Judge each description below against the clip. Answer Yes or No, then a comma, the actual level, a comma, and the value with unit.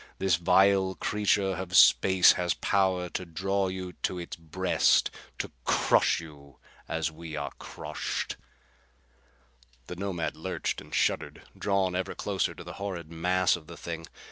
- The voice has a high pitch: No, very low, 90 Hz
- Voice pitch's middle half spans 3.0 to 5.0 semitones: No, narrow, 2.4 semitones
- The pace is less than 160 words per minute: Yes, average, 145 wpm